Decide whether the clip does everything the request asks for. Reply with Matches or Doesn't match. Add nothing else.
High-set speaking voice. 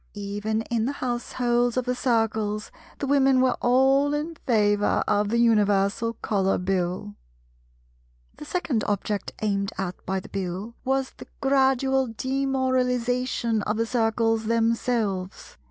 Matches